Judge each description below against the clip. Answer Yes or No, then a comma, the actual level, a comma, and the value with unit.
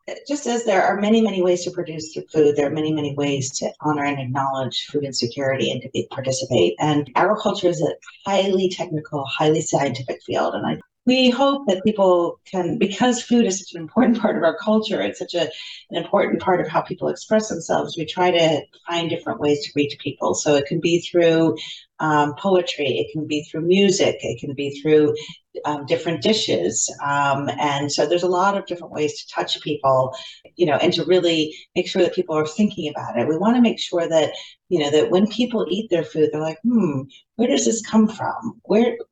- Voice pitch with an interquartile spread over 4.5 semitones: Yes, average, 4.9 semitones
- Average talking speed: No, fast, 210 wpm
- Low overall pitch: No, medium, 165 Hz